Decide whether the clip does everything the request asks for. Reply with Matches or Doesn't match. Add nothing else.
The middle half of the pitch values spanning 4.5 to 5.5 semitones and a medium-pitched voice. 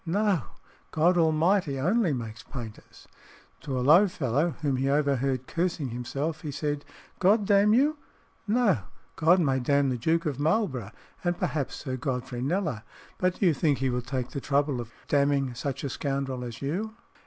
Matches